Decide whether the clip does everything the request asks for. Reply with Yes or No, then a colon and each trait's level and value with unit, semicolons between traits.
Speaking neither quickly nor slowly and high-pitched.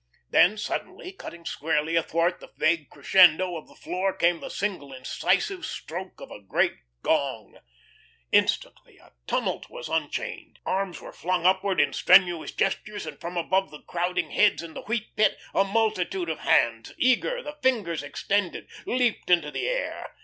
No: average, 160 wpm; medium, 180 Hz